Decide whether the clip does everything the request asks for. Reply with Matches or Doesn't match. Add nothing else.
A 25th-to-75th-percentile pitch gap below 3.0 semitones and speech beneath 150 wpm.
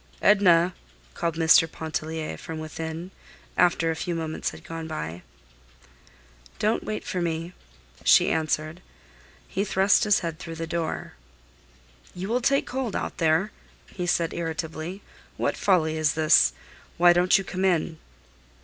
Matches